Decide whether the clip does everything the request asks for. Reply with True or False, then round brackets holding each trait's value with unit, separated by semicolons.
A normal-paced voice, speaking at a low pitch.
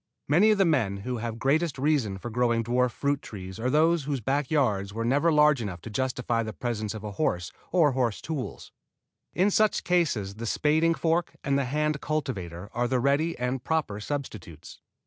True (190 wpm; 130 Hz)